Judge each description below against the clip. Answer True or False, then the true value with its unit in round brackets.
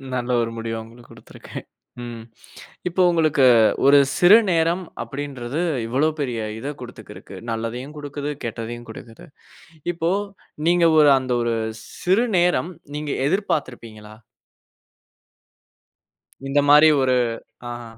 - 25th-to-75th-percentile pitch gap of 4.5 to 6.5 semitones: True (4.9 semitones)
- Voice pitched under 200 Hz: True (135 Hz)